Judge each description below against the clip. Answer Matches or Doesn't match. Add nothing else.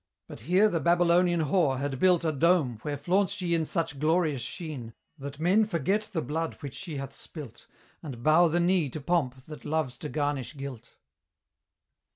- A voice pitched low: Doesn't match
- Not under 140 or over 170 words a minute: Doesn't match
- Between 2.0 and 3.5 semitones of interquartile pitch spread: Doesn't match